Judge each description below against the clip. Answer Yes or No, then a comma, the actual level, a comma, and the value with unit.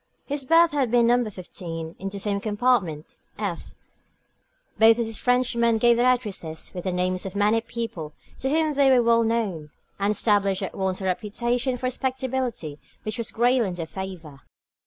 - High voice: Yes, high, 220 Hz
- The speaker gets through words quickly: No, average, 175 wpm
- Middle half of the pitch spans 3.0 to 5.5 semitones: Yes, average, 4.6 semitones